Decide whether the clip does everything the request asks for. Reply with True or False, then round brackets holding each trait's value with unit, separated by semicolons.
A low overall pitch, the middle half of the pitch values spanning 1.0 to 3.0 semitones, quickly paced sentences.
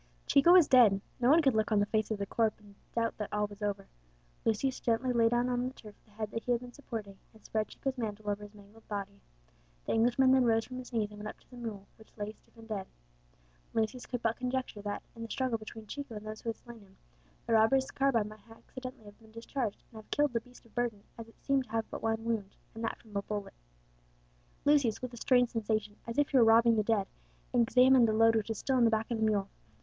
False (225 Hz; 2.6 semitones; 255 wpm)